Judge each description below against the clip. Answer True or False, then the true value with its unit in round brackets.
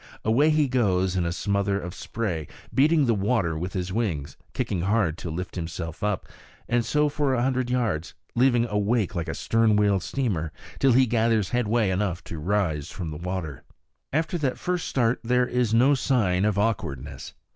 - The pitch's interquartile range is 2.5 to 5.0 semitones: False (5.5 semitones)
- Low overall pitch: True (105 Hz)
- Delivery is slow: False (185 wpm)